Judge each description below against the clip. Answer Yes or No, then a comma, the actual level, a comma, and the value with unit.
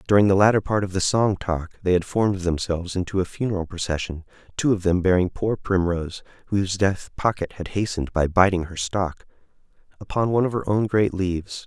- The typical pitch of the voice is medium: No, very low, 95 Hz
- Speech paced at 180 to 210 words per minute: Yes, average, 195 wpm